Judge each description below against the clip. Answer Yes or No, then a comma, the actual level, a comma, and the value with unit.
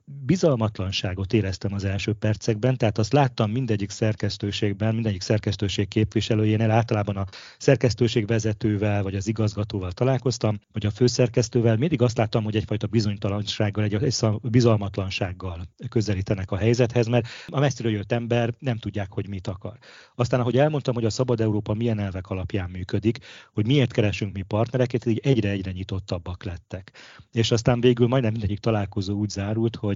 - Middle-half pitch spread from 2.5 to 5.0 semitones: Yes, average, 2.9 semitones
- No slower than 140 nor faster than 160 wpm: Yes, average, 150 wpm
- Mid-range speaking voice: No, low, 110 Hz